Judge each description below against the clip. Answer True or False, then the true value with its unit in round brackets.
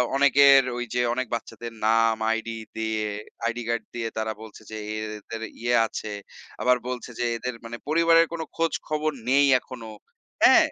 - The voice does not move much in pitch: False (3.7 semitones)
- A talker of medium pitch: False (120 Hz)